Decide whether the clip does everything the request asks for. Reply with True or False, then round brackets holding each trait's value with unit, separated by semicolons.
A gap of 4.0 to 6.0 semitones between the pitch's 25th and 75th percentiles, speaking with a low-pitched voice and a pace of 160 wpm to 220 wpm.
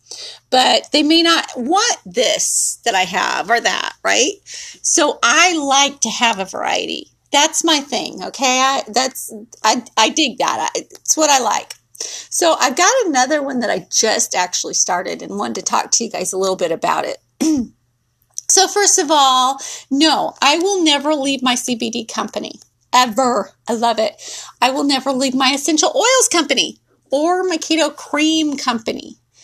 False (4.8 semitones; 270 Hz; 170 wpm)